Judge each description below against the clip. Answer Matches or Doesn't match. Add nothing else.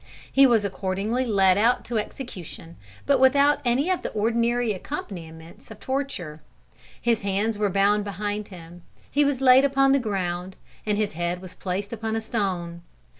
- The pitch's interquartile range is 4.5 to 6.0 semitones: Matches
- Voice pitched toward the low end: Doesn't match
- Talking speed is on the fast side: Doesn't match